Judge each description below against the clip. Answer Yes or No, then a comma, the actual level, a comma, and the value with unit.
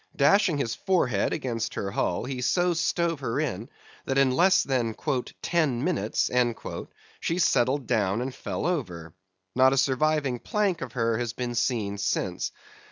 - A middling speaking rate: Yes, average, 155 wpm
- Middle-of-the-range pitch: No, low, 130 Hz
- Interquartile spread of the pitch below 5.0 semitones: No, average, 5.3 semitones